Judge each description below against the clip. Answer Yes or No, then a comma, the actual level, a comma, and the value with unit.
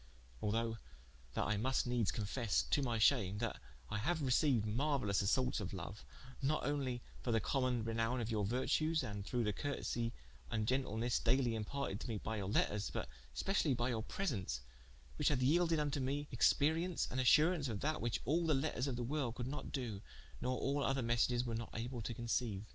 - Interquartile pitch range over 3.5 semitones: Yes, average, 3.9 semitones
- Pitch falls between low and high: No, low, 125 Hz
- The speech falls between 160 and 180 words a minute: No, average, 195 wpm